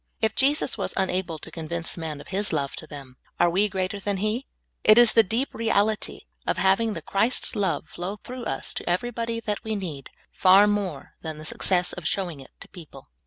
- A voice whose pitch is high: Yes, high, 195 Hz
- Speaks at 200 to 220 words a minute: Yes, fast, 205 wpm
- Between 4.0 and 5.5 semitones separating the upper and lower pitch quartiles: Yes, average, 4.5 semitones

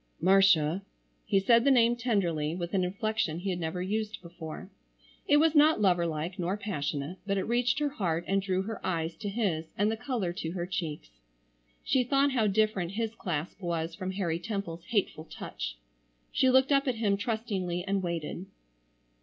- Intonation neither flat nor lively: Yes, average, 4.5 semitones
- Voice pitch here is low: No, high, 195 Hz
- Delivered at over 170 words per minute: Yes, average, 180 wpm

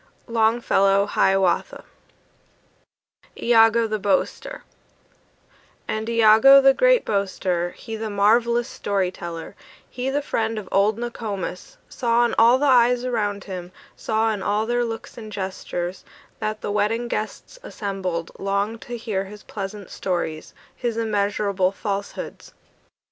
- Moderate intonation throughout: Yes, average, 3.0 semitones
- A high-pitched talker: Yes, high, 215 Hz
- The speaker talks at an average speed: No, slow, 130 wpm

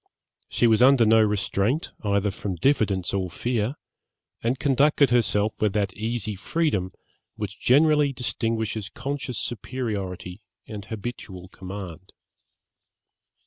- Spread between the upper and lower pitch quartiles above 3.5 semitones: Yes, average, 4.2 semitones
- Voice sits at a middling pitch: No, low, 110 Hz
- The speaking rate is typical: No, slow, 110 wpm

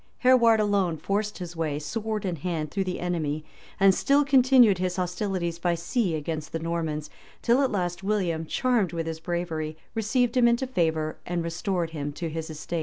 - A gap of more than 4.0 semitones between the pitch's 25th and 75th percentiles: Yes, average, 4.7 semitones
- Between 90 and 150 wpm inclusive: No, average, 180 wpm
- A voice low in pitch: No, medium, 175 Hz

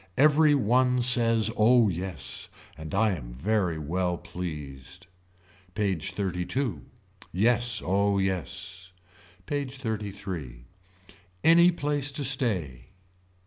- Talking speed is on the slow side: Yes, slow, 100 wpm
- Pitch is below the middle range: Yes, low, 100 Hz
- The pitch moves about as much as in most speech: No, wide, 5.9 semitones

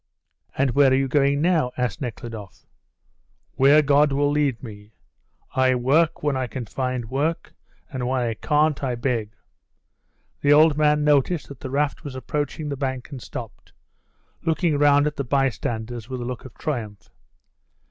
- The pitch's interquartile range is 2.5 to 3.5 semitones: Yes, average, 3.0 semitones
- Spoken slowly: No, average, 165 wpm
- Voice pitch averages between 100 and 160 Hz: Yes, low, 135 Hz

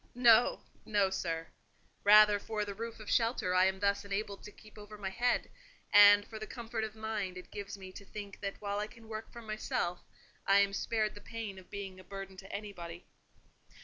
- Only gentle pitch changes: Yes, narrow, 1.9 semitones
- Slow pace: No, average, 200 wpm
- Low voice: No, high, 205 Hz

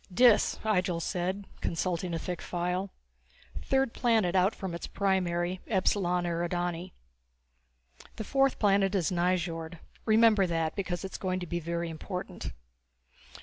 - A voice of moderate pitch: Yes, medium, 180 Hz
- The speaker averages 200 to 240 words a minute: No, average, 140 wpm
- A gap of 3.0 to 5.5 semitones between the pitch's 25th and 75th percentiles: No, narrow, 2.4 semitones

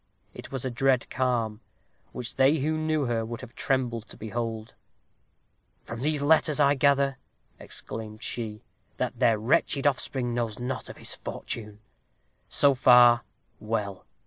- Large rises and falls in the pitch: No, average, 3.4 semitones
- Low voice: Yes, low, 125 Hz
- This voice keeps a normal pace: Yes, average, 145 wpm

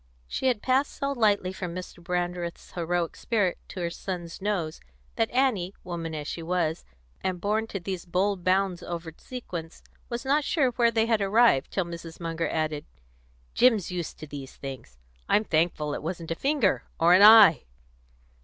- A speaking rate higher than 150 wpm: Yes, average, 170 wpm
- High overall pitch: No, medium, 180 Hz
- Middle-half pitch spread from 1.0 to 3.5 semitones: No, average, 4.6 semitones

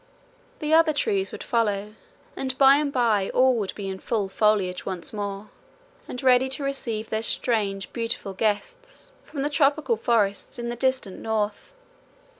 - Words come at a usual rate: Yes, average, 160 wpm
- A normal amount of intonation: Yes, average, 4.8 semitones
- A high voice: Yes, high, 230 Hz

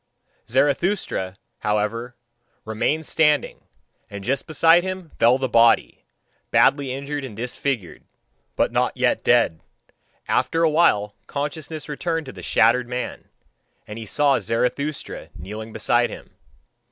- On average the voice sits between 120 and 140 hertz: Yes, low, 135 Hz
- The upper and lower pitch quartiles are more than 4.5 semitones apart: Yes, average, 5.1 semitones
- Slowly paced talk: Yes, slow, 125 wpm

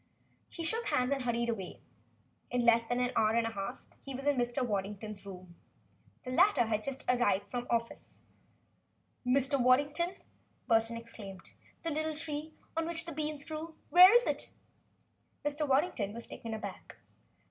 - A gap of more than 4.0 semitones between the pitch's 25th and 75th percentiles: Yes, average, 5.0 semitones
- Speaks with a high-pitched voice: Yes, very high, 250 Hz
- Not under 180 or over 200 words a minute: No, average, 165 wpm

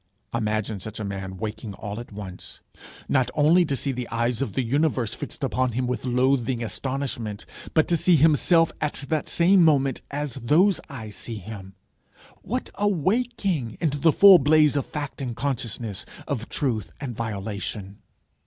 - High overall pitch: No, low, 130 Hz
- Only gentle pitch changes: No, average, 5.3 semitones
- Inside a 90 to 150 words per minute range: No, average, 165 wpm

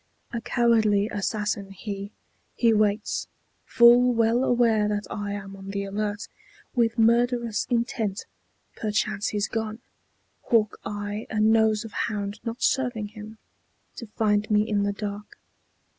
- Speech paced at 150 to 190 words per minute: No, slow, 135 wpm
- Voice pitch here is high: Yes, high, 215 Hz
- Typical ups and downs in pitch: No, narrow, 1.9 semitones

